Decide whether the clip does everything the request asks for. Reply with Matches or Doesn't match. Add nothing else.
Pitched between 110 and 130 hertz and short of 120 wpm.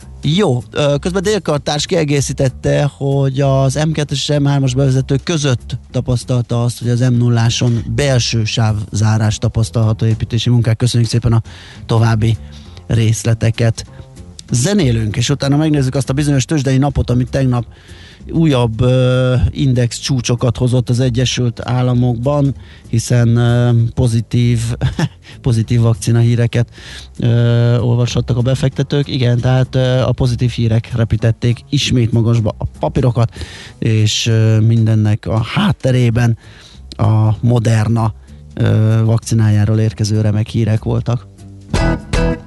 Matches